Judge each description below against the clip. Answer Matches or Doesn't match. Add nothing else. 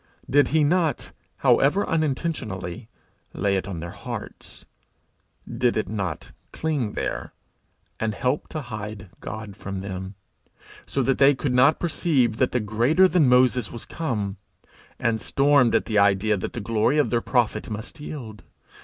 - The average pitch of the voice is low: Matches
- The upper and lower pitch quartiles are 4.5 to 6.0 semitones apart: Matches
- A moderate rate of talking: Matches